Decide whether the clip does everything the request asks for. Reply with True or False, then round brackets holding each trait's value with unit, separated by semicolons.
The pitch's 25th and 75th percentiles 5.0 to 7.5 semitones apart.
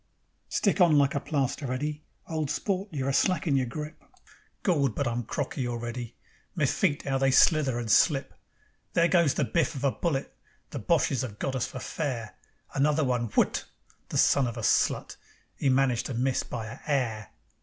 False (3.6 semitones)